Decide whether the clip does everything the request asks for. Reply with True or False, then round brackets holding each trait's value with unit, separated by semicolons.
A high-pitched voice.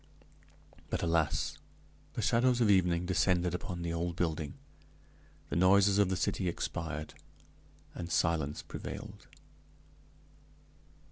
False (85 Hz)